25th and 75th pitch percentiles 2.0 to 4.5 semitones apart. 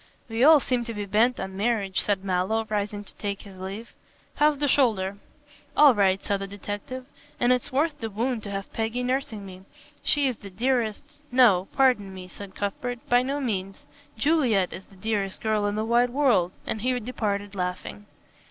Yes: average, 4.0 semitones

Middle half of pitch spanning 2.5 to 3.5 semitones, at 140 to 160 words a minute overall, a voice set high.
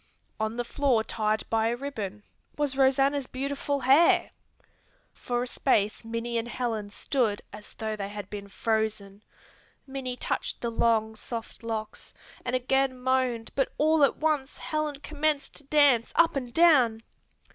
No: average, 4.0 semitones; average, 150 wpm; high, 245 Hz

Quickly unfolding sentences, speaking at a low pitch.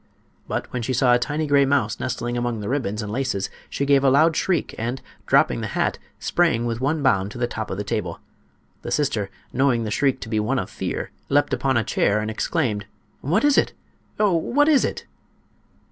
Yes: fast, 210 wpm; low, 125 Hz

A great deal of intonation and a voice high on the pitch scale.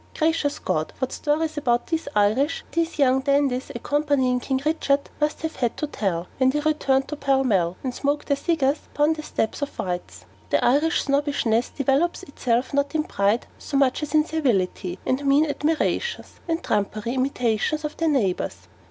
No: average, 3.8 semitones; very high, 275 Hz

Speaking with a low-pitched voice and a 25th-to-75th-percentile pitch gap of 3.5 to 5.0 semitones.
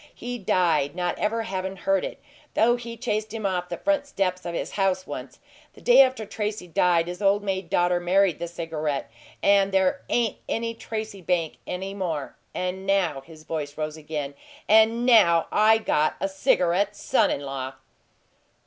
No: high, 190 Hz; average, 4.1 semitones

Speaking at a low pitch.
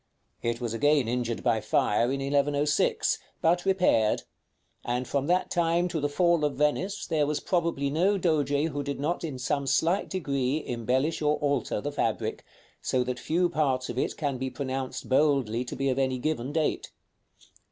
No: medium, 145 Hz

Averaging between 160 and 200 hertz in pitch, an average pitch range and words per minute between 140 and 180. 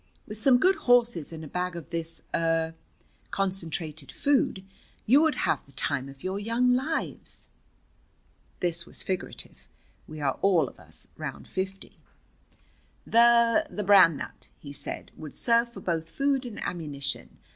No: high, 190 Hz; wide, 6.7 semitones; average, 150 wpm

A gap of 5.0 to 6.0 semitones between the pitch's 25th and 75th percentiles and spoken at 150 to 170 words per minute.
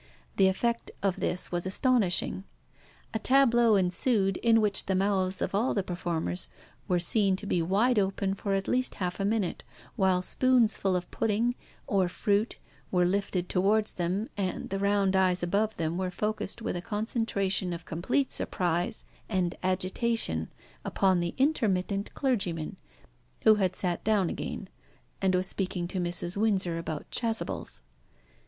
No: average, 3.2 semitones; average, 155 wpm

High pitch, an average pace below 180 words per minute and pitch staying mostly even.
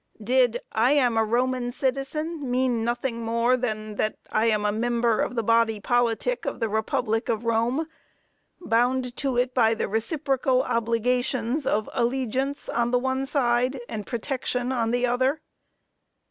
Yes: high, 245 Hz; average, 155 wpm; narrow, 2.2 semitones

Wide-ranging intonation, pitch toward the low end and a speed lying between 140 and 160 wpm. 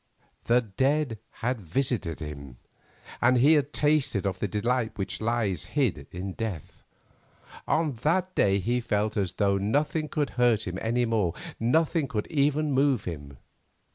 Yes: wide, 6.1 semitones; low, 115 Hz; average, 150 wpm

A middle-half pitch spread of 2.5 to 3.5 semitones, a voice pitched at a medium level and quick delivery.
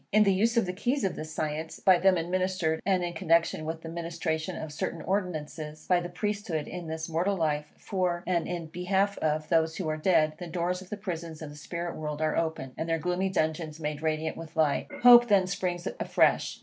Yes: average, 2.8 semitones; medium, 170 Hz; fast, 215 wpm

